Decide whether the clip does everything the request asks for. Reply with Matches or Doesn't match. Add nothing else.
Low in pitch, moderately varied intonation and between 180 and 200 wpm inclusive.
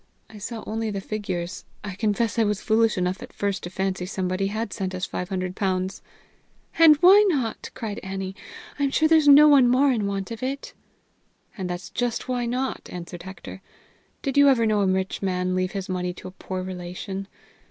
Doesn't match